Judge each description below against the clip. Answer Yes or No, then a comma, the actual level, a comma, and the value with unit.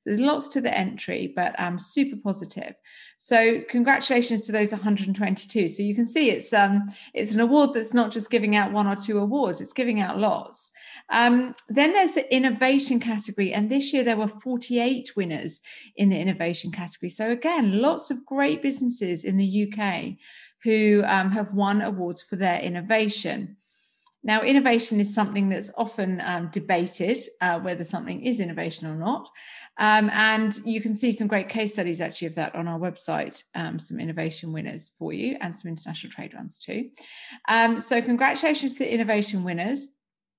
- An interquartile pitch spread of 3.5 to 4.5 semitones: Yes, average, 4.2 semitones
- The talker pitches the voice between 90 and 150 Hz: No, high, 215 Hz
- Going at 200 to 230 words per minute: No, average, 180 wpm